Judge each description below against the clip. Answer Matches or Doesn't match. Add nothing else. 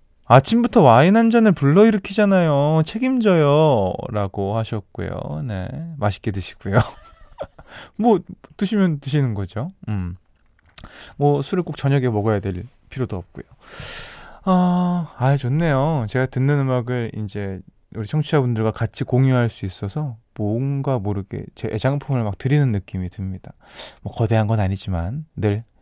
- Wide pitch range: Matches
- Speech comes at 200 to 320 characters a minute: Matches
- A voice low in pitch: Matches